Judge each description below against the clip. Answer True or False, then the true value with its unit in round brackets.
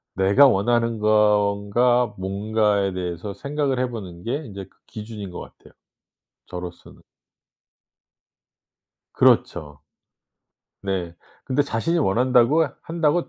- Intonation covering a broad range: False (4.5 semitones)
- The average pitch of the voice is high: False (105 Hz)